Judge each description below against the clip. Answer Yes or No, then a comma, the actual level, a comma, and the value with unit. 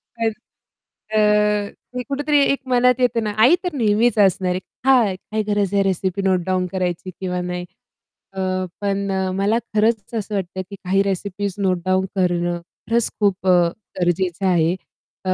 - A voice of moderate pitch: No, high, 195 Hz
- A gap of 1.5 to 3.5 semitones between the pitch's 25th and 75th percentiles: Yes, average, 3.0 semitones